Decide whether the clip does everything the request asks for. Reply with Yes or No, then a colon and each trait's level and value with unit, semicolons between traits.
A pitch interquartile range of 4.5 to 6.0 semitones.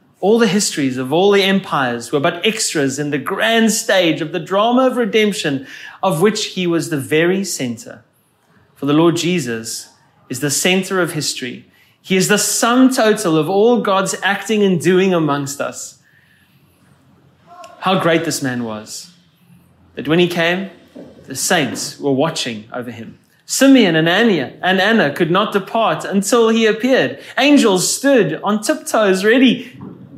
Yes: wide, 5.6 semitones